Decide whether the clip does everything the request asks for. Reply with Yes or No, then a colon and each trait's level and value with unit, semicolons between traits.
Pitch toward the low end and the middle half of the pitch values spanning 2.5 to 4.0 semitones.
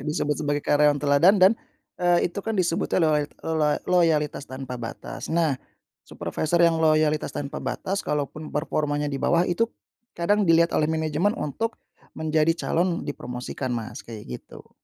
No: medium, 155 Hz; average, 2.8 semitones